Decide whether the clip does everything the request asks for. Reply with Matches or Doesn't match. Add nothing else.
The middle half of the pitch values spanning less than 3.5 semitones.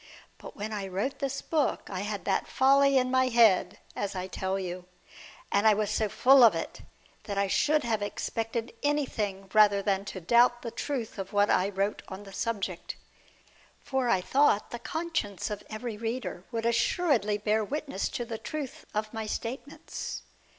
Doesn't match